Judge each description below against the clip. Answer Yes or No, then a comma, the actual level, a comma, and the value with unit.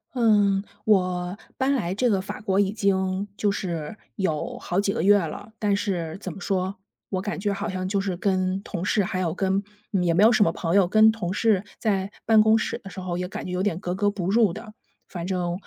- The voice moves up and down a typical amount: No, narrow, 2.2 semitones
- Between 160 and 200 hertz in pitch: Yes, high, 195 Hz